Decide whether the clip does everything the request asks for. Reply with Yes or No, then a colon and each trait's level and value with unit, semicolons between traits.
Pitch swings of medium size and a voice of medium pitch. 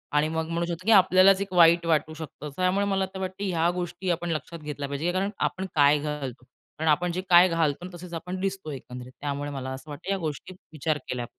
Yes: average, 3.8 semitones; medium, 165 Hz